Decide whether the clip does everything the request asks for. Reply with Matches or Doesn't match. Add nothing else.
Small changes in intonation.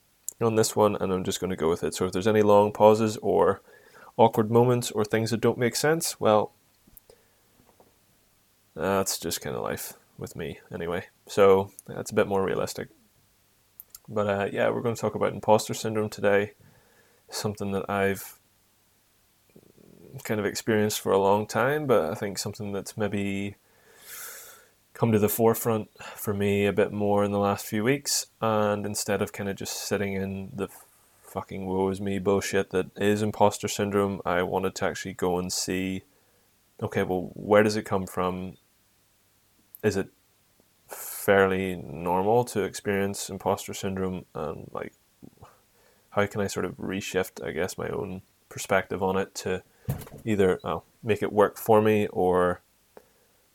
Matches